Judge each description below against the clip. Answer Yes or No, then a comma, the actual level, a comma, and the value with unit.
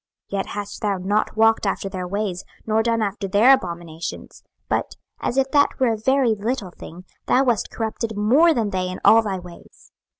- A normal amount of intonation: Yes, average, 3.5 semitones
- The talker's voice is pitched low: No, high, 210 Hz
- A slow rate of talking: No, average, 195 wpm